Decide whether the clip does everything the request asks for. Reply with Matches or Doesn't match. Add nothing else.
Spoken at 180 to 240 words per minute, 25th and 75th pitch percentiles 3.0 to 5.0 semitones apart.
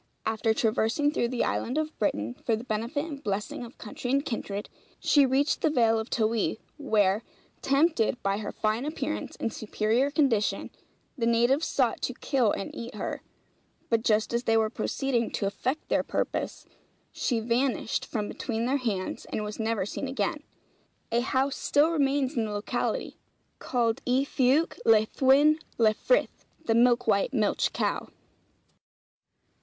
Doesn't match